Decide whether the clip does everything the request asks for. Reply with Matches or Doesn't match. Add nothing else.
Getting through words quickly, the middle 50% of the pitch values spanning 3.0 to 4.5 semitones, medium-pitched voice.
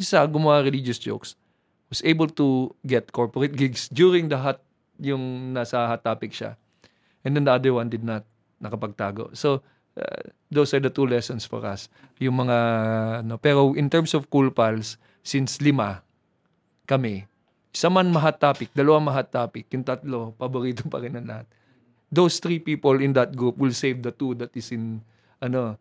Doesn't match